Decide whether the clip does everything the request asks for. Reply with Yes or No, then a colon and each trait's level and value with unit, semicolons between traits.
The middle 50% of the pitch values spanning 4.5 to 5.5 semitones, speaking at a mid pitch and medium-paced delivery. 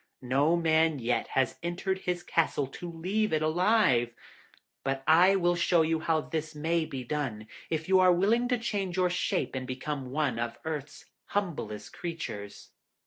Yes: average, 4.8 semitones; medium, 160 Hz; average, 165 wpm